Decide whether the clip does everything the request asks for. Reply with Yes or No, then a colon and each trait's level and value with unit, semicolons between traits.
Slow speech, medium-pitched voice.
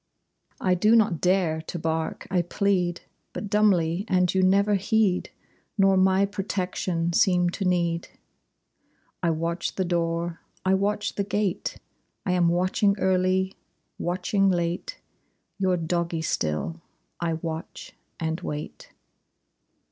Yes: slow, 125 wpm; medium, 180 Hz